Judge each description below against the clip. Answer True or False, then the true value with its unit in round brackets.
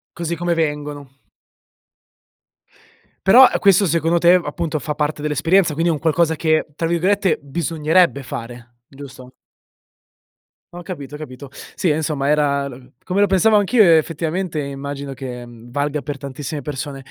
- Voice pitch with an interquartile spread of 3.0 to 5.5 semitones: True (3.4 semitones)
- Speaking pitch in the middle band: True (150 Hz)